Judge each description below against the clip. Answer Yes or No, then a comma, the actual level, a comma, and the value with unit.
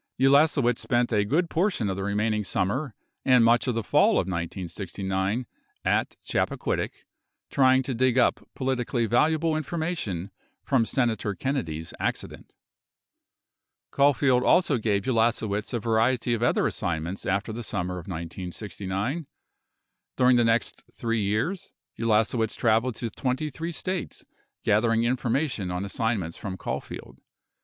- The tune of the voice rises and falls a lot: No, average, 4.5 semitones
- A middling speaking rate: No, slow, 130 wpm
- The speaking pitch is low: Yes, low, 115 Hz